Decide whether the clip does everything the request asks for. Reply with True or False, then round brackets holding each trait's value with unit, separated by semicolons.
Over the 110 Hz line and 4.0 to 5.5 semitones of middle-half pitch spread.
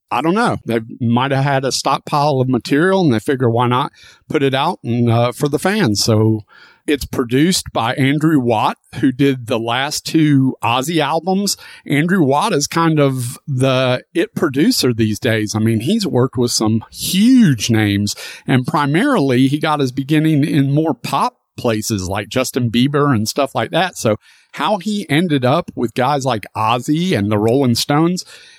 True (135 Hz; 4.4 semitones)